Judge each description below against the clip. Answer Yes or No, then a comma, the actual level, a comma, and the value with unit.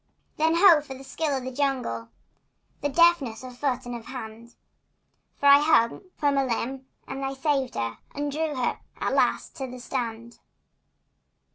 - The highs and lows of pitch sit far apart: No, average, 3.0 semitones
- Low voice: No, very high, 265 Hz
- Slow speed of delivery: No, average, 170 wpm